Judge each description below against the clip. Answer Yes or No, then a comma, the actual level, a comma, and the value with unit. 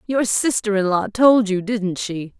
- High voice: Yes, high, 205 Hz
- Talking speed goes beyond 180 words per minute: Yes, average, 200 wpm